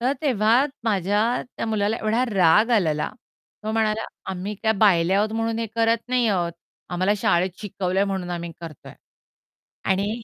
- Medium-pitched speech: No, high, 205 Hz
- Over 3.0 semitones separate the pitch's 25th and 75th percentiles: Yes, average, 3.5 semitones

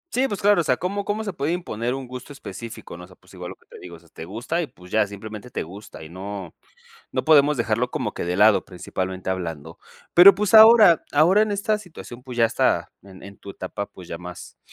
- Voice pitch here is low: Yes, low, 115 Hz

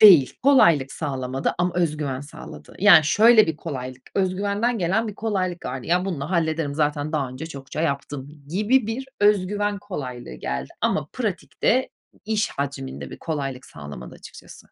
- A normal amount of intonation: No, wide, 6.8 semitones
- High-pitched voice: No, medium, 160 Hz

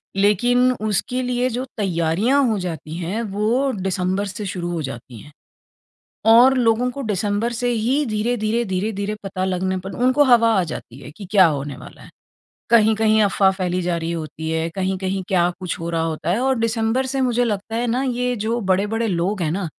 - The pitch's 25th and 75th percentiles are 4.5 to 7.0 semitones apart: Yes, average, 4.8 semitones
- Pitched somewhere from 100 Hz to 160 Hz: No, high, 205 Hz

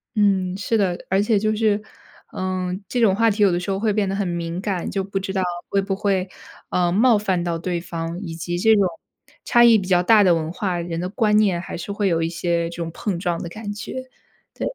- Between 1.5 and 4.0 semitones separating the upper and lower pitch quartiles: Yes, average, 3.1 semitones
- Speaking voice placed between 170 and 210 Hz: Yes, high, 190 Hz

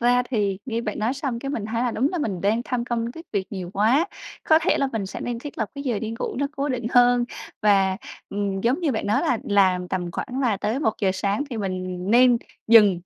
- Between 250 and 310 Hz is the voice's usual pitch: No, high, 230 Hz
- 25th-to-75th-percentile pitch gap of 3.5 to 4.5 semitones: Yes, average, 3.9 semitones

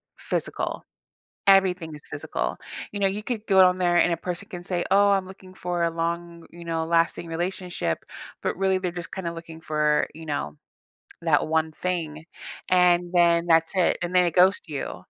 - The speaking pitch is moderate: Yes, medium, 175 Hz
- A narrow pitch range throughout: Yes, narrow, 2.2 semitones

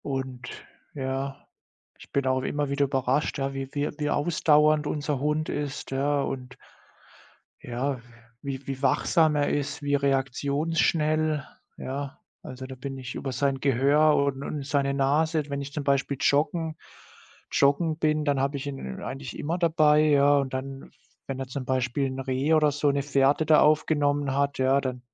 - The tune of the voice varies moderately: No, narrow, 1.8 semitones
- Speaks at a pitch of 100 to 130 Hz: No, medium, 140 Hz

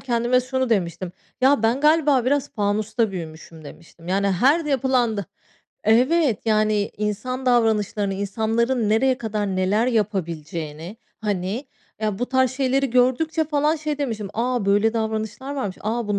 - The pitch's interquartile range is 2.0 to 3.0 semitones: No, average, 4.3 semitones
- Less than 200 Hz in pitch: No, high, 225 Hz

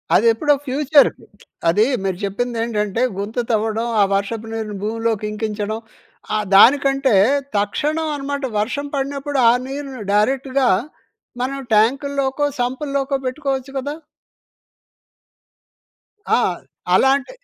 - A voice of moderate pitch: No, very high, 255 Hz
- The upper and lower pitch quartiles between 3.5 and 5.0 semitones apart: Yes, average, 4.3 semitones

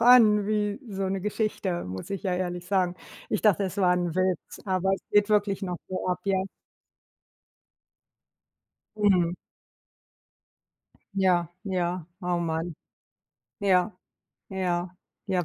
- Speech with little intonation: Yes, narrow, 2.2 semitones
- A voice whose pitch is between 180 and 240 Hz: Yes, medium, 185 Hz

